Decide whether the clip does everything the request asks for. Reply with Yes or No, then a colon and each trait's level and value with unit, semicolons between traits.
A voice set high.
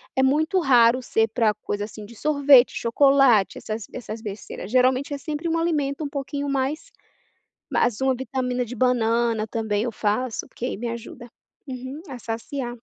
Yes: very high, 250 Hz